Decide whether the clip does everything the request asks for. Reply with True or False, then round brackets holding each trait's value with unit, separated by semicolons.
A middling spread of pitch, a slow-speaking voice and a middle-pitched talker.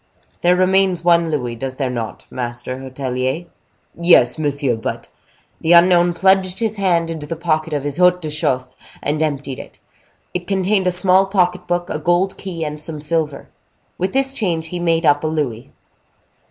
False (3.9 semitones; 175 wpm; 165 Hz)